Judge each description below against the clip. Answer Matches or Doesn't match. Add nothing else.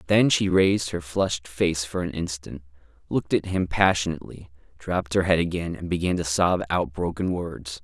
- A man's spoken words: Matches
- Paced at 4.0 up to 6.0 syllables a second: Matches